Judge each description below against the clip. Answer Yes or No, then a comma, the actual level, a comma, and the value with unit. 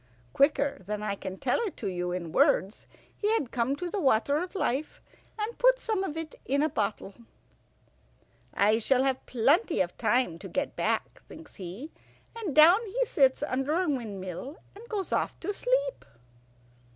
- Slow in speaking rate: No, average, 170 wpm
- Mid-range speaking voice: No, very high, 280 Hz